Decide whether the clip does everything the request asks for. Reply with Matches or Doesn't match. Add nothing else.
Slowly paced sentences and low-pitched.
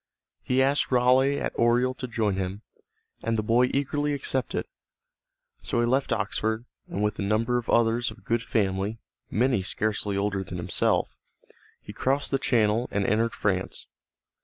Doesn't match